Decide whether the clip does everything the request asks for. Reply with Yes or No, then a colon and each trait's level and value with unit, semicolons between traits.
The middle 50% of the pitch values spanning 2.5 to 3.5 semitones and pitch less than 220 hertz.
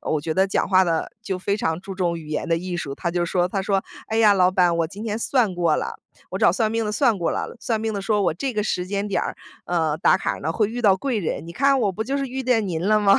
No: average, 4.0 semitones; high, 195 Hz